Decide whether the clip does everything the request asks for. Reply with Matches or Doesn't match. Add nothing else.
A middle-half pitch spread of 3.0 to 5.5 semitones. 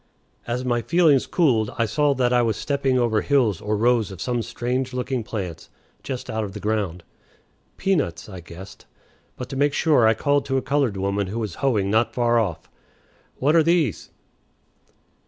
Matches